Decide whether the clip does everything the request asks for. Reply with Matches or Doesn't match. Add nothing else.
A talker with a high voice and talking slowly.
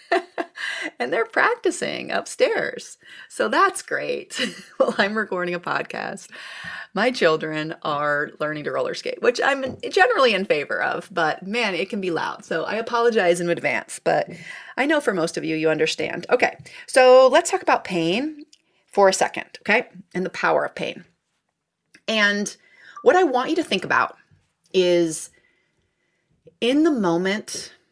Doesn't match